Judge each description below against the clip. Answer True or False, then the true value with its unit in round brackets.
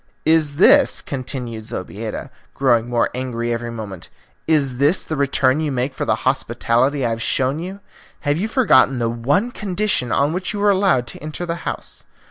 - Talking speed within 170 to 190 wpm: True (180 wpm)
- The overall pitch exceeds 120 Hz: True (140 Hz)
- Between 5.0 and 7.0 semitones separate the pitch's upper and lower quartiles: True (5.3 semitones)